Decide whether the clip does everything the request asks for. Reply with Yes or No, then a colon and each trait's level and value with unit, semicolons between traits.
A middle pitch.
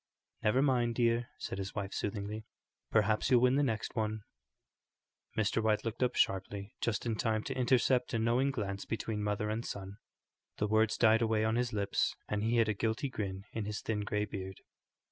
No: low, 110 Hz